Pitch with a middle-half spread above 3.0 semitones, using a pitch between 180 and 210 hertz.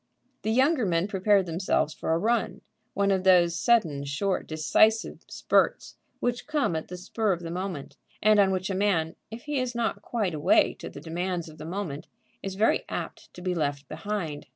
Yes: average, 4.5 semitones; medium, 185 Hz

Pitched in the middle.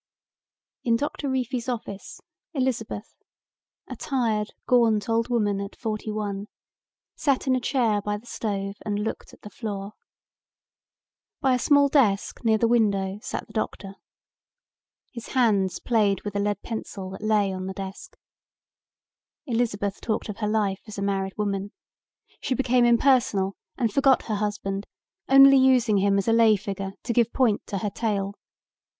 No: high, 215 Hz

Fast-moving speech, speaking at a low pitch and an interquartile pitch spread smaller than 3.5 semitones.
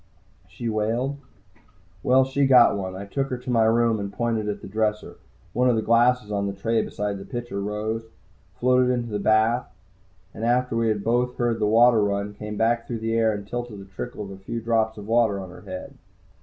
Yes: fast, 210 wpm; low, 110 Hz; average, 2.7 semitones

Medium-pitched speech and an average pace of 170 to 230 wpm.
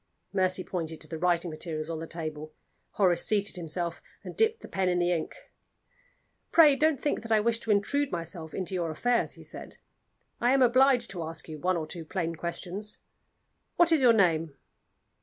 Yes: medium, 180 Hz; average, 190 wpm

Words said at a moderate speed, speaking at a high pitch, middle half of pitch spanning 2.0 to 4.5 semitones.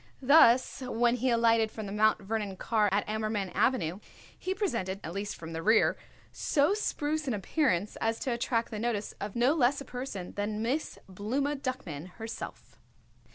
Yes: average, 170 wpm; high, 225 Hz; average, 4.1 semitones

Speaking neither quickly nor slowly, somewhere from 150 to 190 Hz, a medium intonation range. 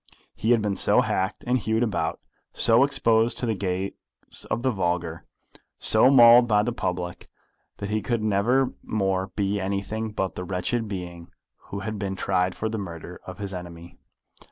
No: average, 175 wpm; low, 100 Hz; average, 3.3 semitones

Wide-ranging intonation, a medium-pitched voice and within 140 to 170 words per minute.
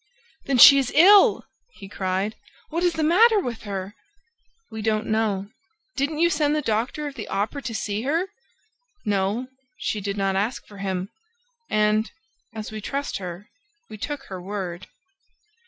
No: wide, 6.1 semitones; high, 220 Hz; average, 160 wpm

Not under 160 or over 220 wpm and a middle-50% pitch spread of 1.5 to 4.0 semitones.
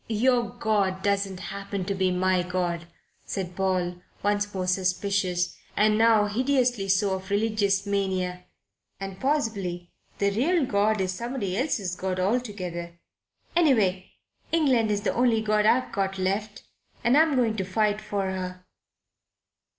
No: slow, 135 wpm; average, 2.9 semitones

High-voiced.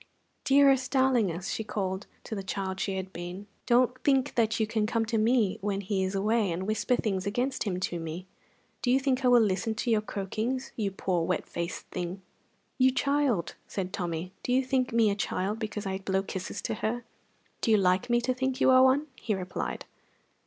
Yes: high, 215 Hz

